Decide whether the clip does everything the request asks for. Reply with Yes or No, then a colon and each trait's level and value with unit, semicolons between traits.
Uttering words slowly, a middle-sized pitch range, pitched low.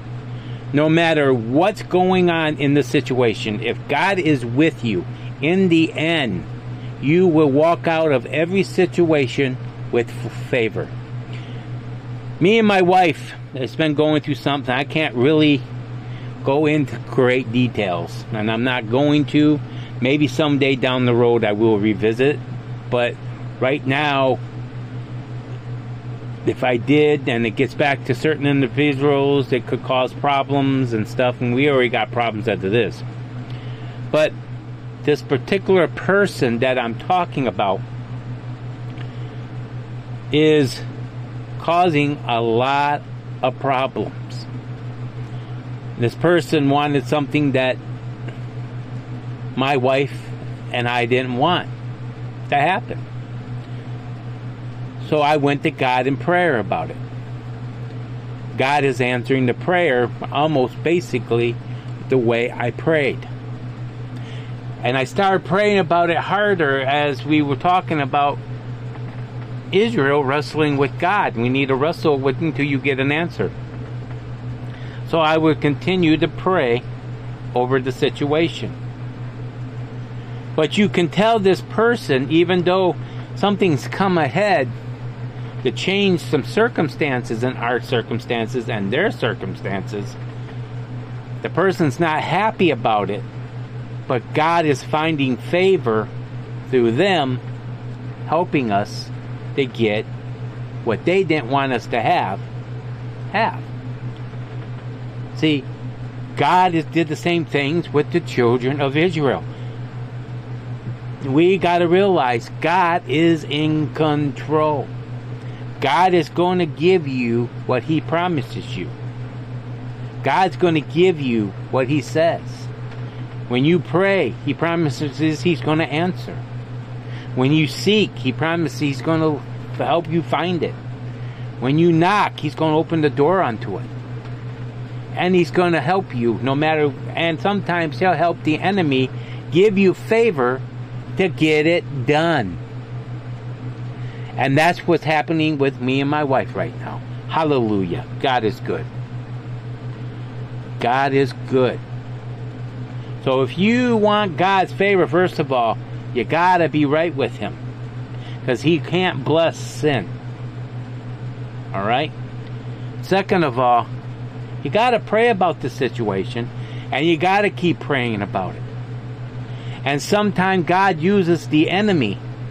Yes: slow, 125 wpm; average, 3.9 semitones; low, 125 Hz